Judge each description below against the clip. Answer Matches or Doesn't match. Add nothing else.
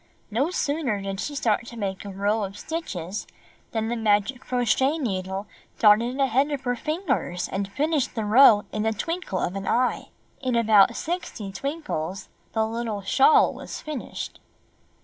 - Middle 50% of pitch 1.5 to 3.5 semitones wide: Doesn't match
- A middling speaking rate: Matches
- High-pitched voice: Matches